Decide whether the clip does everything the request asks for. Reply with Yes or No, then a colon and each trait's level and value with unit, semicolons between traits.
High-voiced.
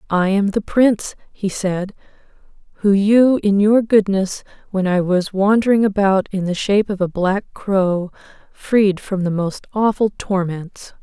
Yes: high, 200 Hz